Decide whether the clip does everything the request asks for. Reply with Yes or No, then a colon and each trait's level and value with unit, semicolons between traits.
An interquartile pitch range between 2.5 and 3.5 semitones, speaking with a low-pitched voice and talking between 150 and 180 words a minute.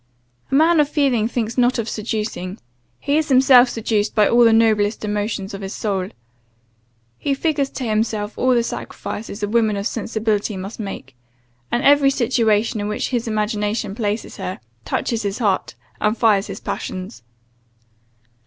No: average, 2.8 semitones; high, 220 Hz; average, 160 wpm